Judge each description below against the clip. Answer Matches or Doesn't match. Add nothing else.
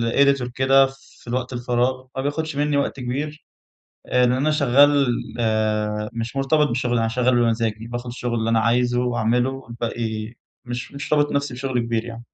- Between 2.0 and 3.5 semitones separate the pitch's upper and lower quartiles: Matches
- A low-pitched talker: Matches